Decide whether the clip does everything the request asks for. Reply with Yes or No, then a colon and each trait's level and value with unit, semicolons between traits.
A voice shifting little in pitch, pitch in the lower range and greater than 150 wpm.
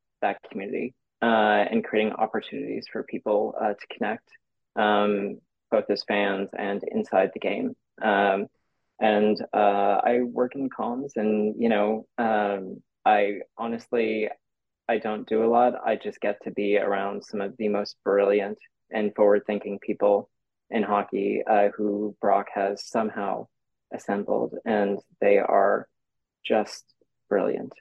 No: narrow, 1.4 semitones; low, 105 Hz; average, 140 wpm